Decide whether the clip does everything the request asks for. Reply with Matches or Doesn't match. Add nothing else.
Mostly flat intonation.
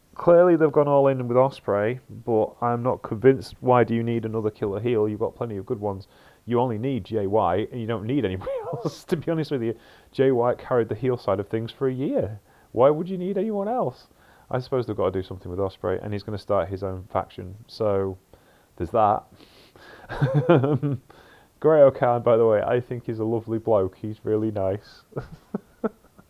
Doesn't match